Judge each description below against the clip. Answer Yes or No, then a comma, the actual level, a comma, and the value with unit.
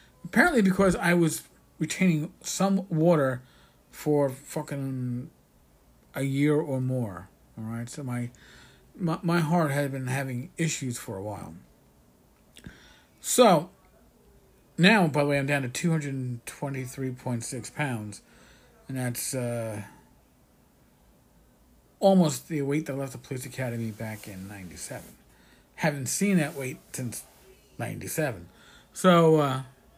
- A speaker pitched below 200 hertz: Yes, low, 135 Hz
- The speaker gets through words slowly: Yes, slow, 120 wpm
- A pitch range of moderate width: Yes, average, 4.4 semitones